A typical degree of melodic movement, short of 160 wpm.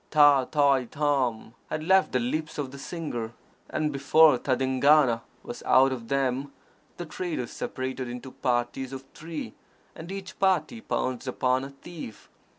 Yes: average, 3.2 semitones; average, 150 wpm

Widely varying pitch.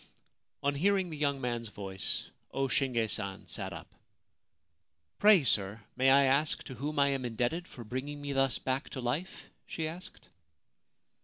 No: average, 3.4 semitones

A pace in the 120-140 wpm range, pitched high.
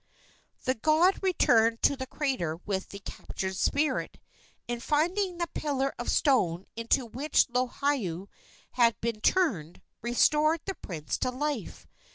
Yes: slow, 135 wpm; very high, 255 Hz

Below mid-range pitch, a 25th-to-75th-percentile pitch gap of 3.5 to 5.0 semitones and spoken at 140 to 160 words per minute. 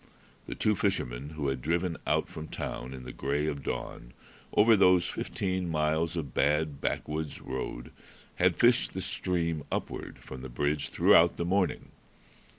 Yes: very low, 75 Hz; average, 4.1 semitones; average, 155 wpm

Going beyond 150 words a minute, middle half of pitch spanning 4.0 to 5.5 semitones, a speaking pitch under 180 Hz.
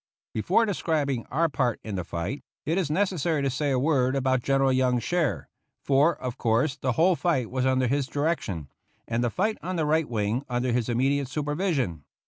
Yes: average, 190 wpm; average, 4.4 semitones; low, 135 Hz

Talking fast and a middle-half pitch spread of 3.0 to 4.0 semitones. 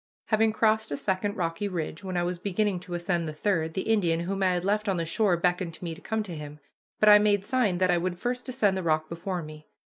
Yes: fast, 260 wpm; average, 3.6 semitones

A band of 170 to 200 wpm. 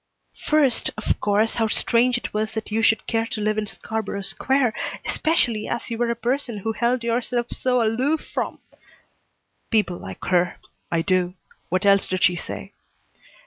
Yes: average, 175 wpm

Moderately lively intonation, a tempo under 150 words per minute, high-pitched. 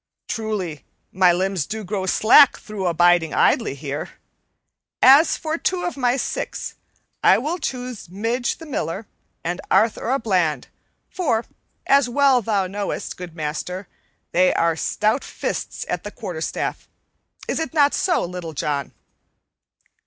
No: wide, 6.3 semitones; average, 140 wpm; high, 205 Hz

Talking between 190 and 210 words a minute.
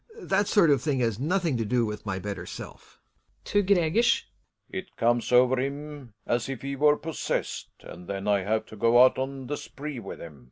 Yes: fast, 205 wpm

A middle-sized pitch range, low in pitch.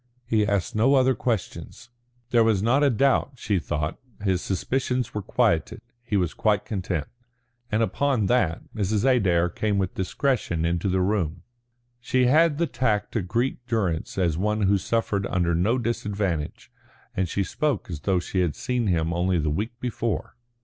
Yes: average, 4.9 semitones; low, 105 Hz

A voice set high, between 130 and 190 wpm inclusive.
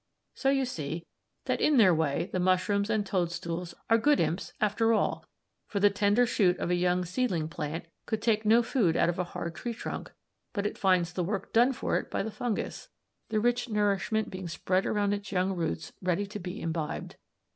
No: high, 195 Hz; average, 200 wpm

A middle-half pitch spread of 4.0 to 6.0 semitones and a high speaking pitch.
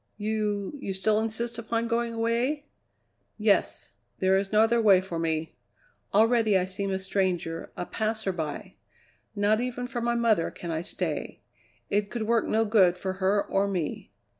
No: average, 3.3 semitones; high, 210 Hz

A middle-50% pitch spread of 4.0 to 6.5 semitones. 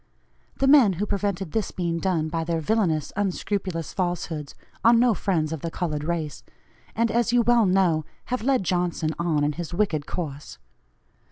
Yes: average, 4.5 semitones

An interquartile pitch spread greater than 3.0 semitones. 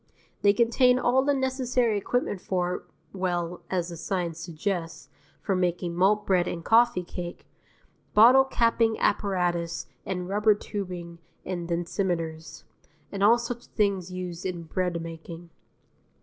Yes: average, 3.9 semitones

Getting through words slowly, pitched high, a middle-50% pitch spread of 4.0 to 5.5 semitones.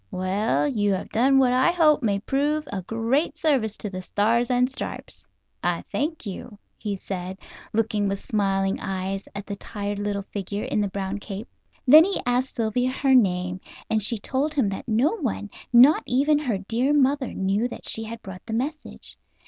No: average, 185 wpm; high, 225 Hz; average, 4.9 semitones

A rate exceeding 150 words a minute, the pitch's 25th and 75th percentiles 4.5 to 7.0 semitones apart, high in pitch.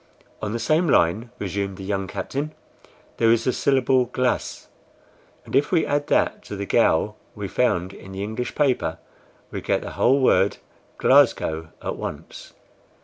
No: average, 160 wpm; average, 5.1 semitones; low, 115 Hz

